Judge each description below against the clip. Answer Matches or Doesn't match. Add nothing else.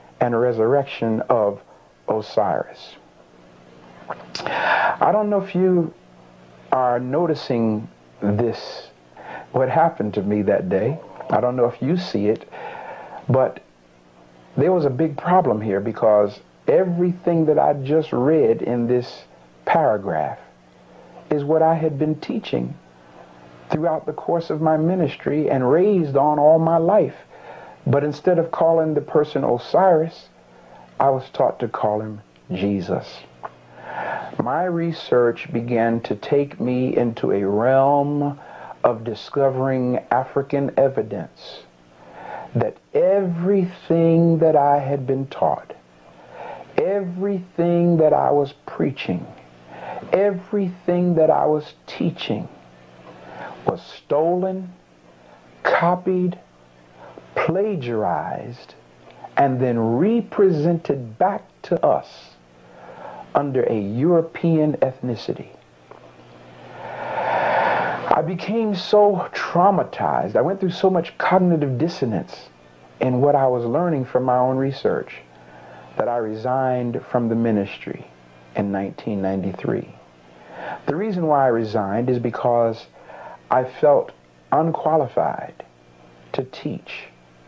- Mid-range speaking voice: Doesn't match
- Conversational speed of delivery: Doesn't match